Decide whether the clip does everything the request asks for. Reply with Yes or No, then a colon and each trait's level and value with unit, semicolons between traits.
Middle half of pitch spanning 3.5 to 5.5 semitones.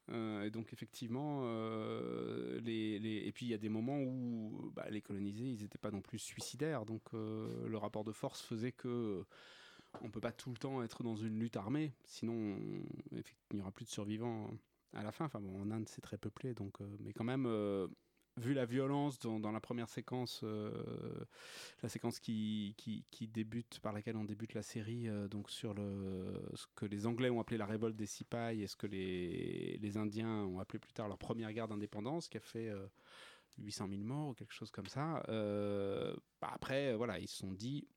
No: narrow, 2.4 semitones